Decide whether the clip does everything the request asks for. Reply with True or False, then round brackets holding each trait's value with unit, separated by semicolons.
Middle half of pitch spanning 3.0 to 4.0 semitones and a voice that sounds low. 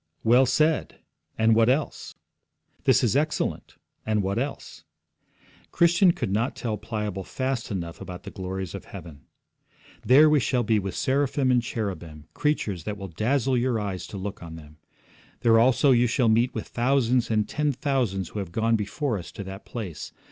False (5.1 semitones; 115 Hz)